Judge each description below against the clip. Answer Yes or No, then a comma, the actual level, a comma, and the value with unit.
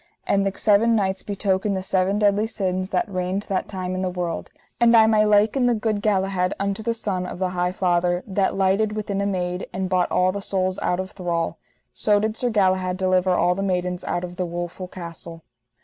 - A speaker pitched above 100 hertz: Yes, high, 190 Hz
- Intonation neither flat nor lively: No, narrow, 2.0 semitones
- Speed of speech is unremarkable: No, fast, 210 wpm